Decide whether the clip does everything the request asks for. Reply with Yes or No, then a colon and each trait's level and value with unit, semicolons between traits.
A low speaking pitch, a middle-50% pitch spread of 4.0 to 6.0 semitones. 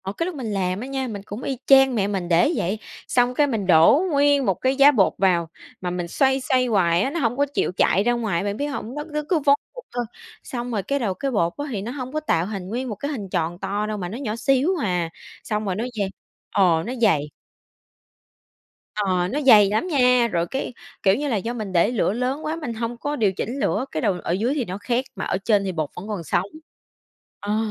No: high, 220 Hz; wide, 5.6 semitones